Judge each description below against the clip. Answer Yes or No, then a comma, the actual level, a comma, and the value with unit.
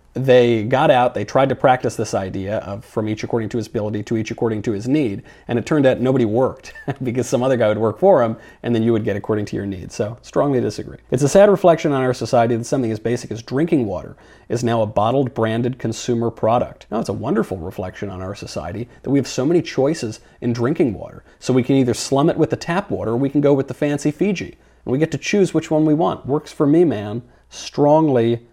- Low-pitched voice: Yes, low, 120 Hz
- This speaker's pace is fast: Yes, fast, 250 wpm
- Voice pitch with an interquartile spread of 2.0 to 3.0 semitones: No, average, 3.7 semitones